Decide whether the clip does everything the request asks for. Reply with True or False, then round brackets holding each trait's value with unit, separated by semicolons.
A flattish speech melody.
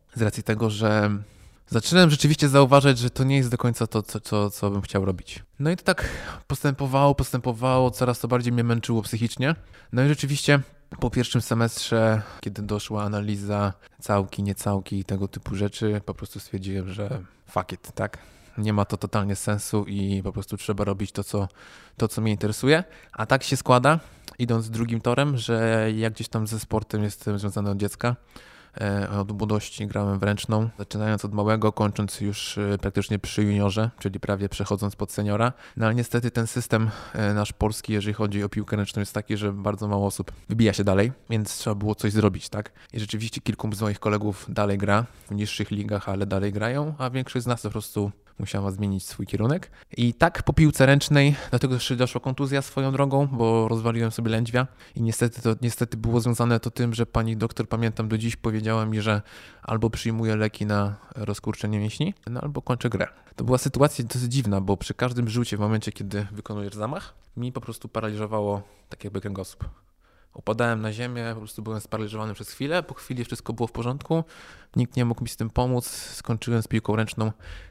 False (3.0 semitones)